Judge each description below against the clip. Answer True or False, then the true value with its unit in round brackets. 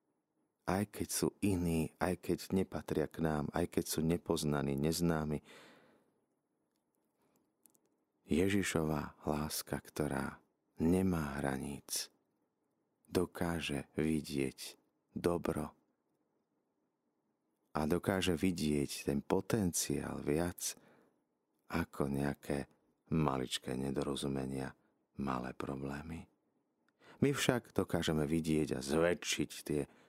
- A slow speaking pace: True (80 wpm)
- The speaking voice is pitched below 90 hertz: True (75 Hz)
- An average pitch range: True (3.5 semitones)